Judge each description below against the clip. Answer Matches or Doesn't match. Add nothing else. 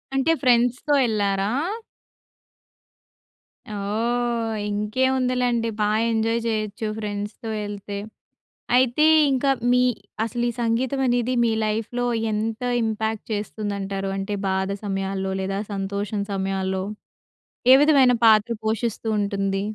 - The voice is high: Matches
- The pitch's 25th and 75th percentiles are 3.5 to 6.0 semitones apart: Doesn't match